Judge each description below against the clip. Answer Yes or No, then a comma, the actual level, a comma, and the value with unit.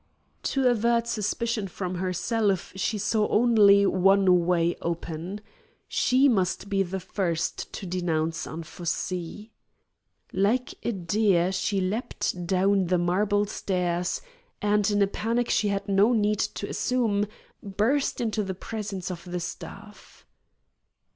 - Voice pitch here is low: No, high, 200 Hz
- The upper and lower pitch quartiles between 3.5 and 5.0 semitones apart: No, average, 2.9 semitones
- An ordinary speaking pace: No, slow, 130 wpm